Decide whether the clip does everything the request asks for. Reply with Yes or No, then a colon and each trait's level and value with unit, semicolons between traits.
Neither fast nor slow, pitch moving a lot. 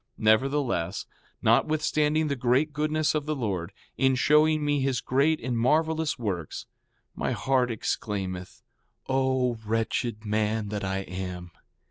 No: slow, 130 wpm; wide, 6.0 semitones